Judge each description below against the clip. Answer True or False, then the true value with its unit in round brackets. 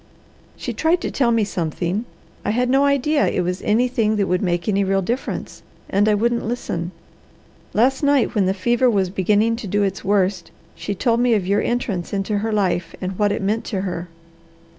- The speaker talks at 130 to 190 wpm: False (200 wpm)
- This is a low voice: False (205 Hz)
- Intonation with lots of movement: False (3.9 semitones)